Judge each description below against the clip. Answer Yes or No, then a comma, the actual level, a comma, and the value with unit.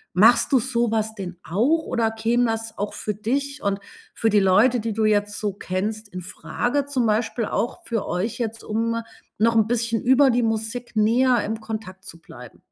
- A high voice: Yes, high, 225 Hz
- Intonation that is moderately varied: No, narrow, 2.3 semitones